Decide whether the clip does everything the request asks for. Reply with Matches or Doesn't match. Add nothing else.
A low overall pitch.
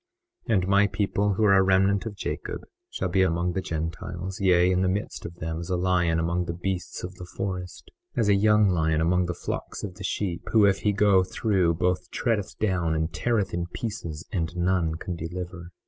Matches